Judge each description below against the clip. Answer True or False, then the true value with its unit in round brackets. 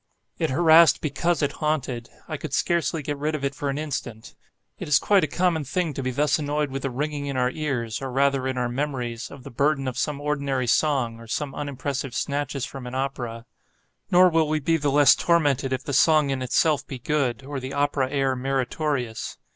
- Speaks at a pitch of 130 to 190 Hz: True (140 Hz)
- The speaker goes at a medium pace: False (210 wpm)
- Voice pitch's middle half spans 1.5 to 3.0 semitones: True (2.5 semitones)